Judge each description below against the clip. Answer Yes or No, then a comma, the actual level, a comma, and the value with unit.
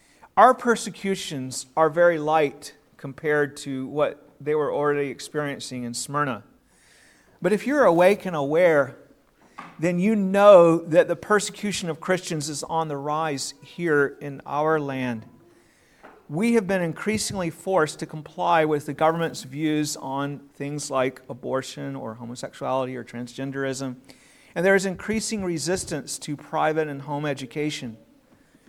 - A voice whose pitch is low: No, medium, 150 Hz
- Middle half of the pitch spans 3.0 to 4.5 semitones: Yes, average, 4.0 semitones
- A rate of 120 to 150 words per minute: Yes, slow, 135 wpm